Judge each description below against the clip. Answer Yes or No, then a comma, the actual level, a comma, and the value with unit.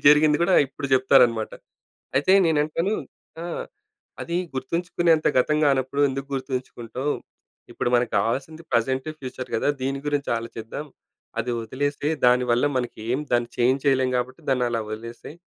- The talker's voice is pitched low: Yes, low, 130 Hz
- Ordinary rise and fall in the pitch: Yes, average, 3.1 semitones